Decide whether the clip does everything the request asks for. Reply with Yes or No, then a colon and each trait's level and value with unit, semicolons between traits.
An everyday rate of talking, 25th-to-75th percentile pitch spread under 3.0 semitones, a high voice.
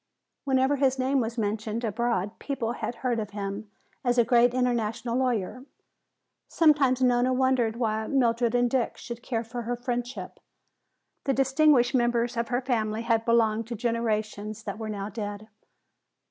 Yes: average, 155 wpm; narrow, 2.4 semitones; high, 235 Hz